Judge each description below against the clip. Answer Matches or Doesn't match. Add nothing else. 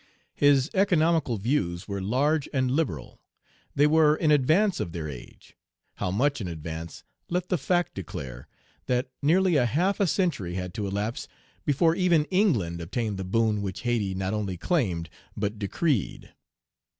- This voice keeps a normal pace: Matches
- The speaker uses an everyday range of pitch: Doesn't match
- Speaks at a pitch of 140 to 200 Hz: Doesn't match